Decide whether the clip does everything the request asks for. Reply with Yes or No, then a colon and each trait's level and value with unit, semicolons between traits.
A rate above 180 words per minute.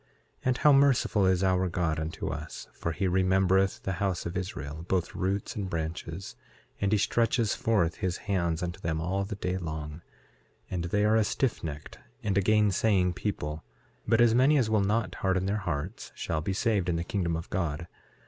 Yes: average, 190 wpm